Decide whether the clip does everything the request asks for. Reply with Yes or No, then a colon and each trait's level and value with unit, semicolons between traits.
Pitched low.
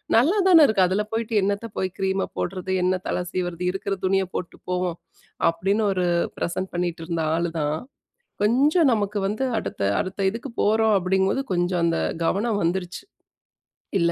No: high, 190 Hz